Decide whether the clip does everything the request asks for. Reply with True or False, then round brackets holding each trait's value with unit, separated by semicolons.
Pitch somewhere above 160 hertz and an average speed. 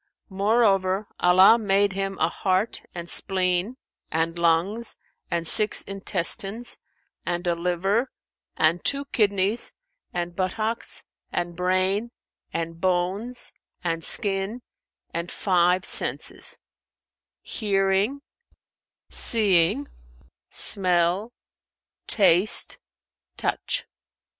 False (190 Hz; 85 wpm)